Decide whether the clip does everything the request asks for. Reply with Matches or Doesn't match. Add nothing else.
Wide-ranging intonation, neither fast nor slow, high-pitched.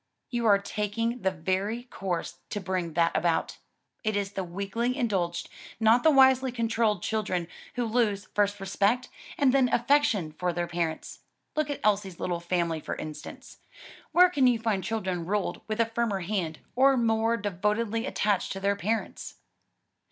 Doesn't match